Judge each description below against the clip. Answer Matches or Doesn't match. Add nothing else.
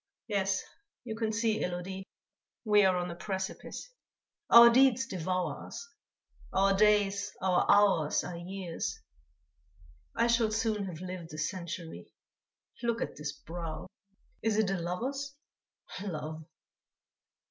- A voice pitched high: Matches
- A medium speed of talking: Doesn't match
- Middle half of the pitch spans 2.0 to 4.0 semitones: Matches